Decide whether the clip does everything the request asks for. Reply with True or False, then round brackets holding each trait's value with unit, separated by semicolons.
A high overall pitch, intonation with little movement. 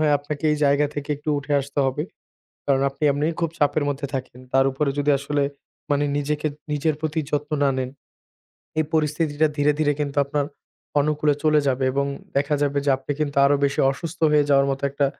False (145 Hz; 1.3 semitones)